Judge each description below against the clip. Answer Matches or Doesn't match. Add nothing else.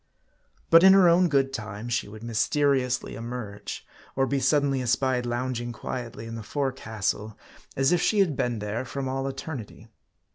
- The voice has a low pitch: Matches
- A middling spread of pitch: Matches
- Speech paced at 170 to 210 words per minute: Doesn't match